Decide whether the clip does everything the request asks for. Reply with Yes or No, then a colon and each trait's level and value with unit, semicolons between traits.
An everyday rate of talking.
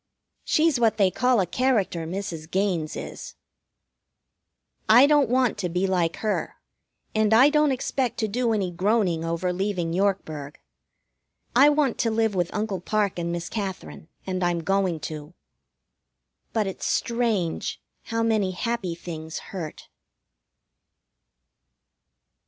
No: slow, 130 wpm